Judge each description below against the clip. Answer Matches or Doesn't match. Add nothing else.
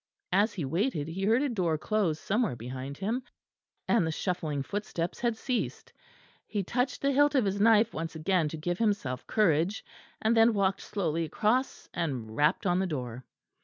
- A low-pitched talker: Doesn't match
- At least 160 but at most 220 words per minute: Matches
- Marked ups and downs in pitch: Matches